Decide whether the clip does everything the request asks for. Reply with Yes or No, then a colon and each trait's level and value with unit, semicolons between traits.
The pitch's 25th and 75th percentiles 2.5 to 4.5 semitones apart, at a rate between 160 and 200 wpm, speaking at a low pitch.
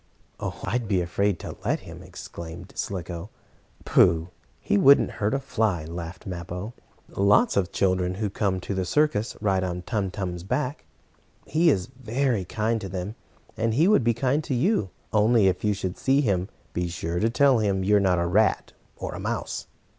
Yes: average, 4.2 semitones; average, 185 wpm; low, 100 Hz